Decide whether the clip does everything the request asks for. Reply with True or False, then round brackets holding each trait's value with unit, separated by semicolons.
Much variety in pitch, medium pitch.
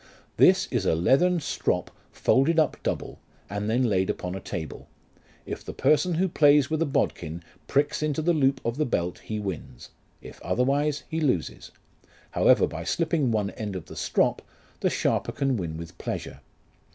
False (8.4 semitones; 130 Hz)